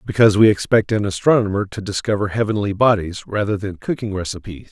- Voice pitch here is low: Yes, low, 100 Hz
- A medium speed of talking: Yes, average, 165 wpm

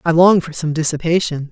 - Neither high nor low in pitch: Yes, medium, 160 Hz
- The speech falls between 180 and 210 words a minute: Yes, average, 200 wpm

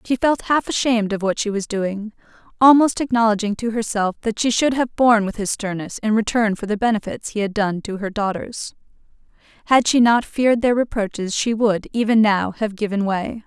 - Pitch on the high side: Yes, high, 220 Hz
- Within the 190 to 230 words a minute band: Yes, average, 200 wpm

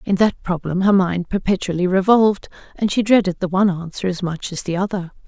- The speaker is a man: No, female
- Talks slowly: No, fast, 205 wpm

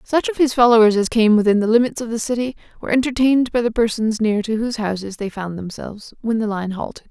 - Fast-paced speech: Yes, fast, 235 wpm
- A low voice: No, high, 225 Hz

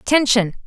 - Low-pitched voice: No, high, 240 Hz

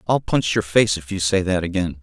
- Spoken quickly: Yes, fast, 265 wpm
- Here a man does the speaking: Yes, male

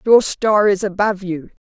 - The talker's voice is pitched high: Yes, high, 200 Hz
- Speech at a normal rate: Yes, average, 180 wpm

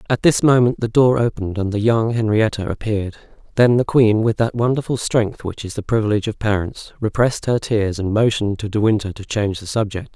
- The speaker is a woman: No, male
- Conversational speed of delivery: No, fast, 215 wpm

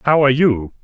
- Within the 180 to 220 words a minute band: Yes, fast, 215 wpm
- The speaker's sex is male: Yes, male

